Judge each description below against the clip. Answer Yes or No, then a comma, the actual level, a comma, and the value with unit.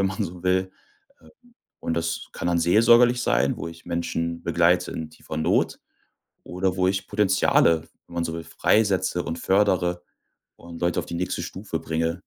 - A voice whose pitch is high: No, very low, 90 Hz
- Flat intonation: Yes, narrow, 2.2 semitones